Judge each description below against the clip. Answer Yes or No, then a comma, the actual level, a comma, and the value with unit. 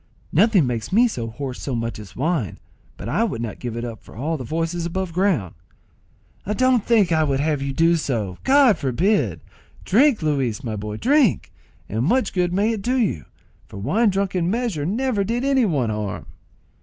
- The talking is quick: No, average, 195 wpm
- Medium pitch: Yes, medium, 165 Hz